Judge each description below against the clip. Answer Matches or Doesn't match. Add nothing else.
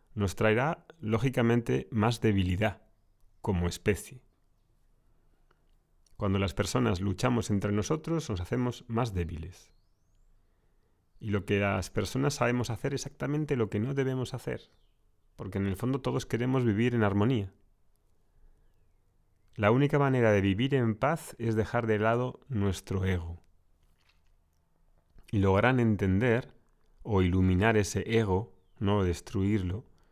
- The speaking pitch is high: Doesn't match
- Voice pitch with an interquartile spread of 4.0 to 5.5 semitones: Matches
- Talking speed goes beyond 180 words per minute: Doesn't match